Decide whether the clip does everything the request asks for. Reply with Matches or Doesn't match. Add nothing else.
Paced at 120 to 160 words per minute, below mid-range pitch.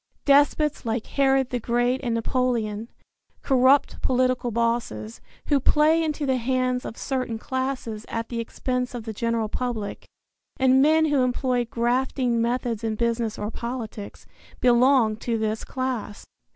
Doesn't match